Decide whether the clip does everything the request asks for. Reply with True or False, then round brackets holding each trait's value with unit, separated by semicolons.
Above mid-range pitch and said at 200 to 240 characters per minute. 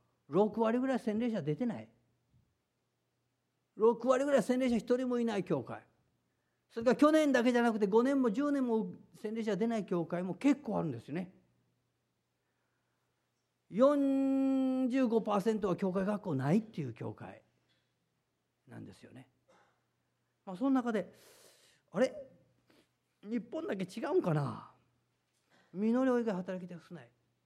True (215 Hz; 235 characters per minute)